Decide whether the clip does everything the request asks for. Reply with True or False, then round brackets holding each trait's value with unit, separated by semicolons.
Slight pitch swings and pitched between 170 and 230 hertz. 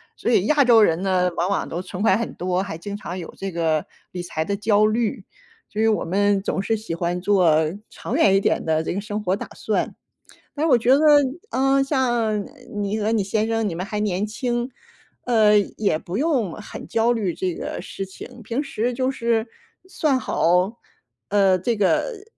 False (4.1 semitones; 210 Hz)